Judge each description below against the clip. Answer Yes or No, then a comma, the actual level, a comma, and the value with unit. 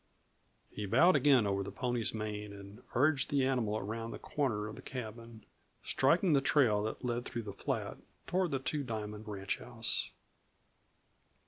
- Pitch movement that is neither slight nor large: Yes, average, 4.1 semitones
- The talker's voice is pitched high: No, low, 115 Hz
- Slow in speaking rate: No, average, 155 wpm